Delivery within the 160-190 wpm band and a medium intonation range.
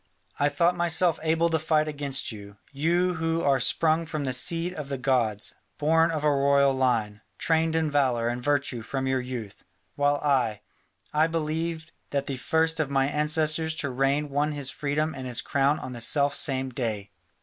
Yes: average, 185 wpm; average, 3.4 semitones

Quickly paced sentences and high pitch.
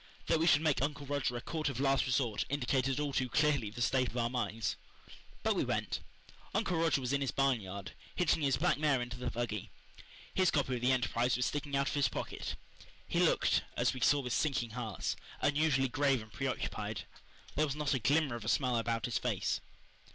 No: fast, 210 wpm; low, 135 Hz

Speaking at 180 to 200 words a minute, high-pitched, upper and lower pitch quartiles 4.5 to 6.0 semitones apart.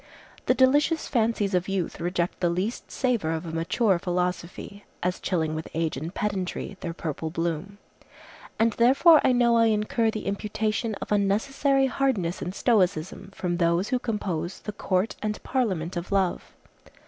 No: average, 160 wpm; high, 195 Hz; average, 4.8 semitones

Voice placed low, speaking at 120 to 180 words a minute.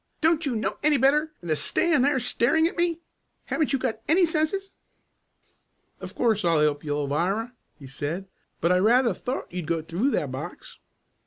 No: high, 235 Hz; average, 175 wpm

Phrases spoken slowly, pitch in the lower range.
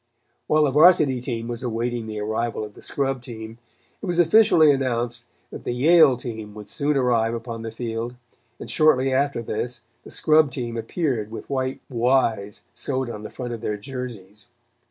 No: average, 175 wpm; low, 120 Hz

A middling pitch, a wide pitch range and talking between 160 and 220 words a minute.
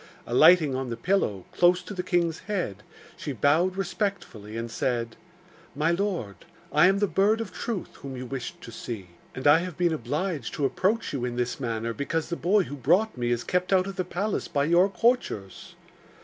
Yes: medium, 160 Hz; wide, 7.2 semitones; average, 195 wpm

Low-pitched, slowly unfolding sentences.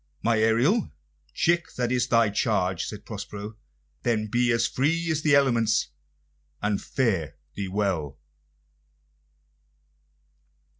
Yes: low, 115 Hz; slow, 105 wpm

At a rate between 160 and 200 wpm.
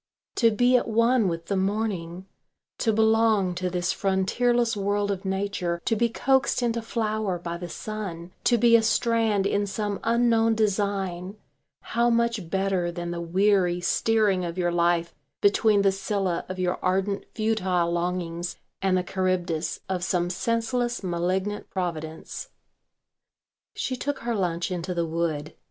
No: average, 150 wpm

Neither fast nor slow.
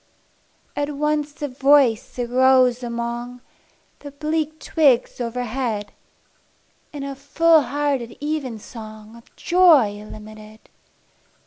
No: slow, 95 wpm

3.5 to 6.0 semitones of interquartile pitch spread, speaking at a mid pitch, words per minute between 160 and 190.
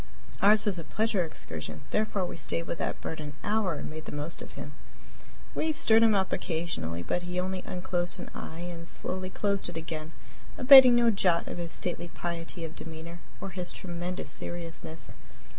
No: average, 2.9 semitones; medium, 175 Hz; average, 185 wpm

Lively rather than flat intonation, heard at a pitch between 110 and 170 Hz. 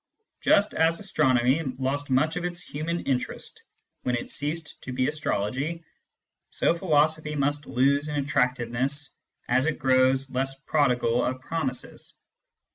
No: average, 3.3 semitones; medium, 140 Hz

